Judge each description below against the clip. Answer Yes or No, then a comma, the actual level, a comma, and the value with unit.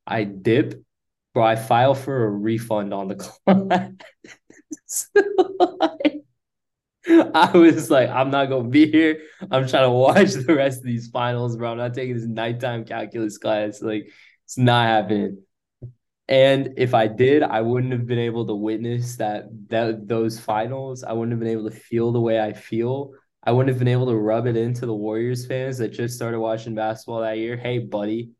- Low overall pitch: Yes, low, 120 Hz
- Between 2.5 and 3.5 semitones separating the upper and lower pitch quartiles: Yes, average, 2.9 semitones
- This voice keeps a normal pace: Yes, average, 190 wpm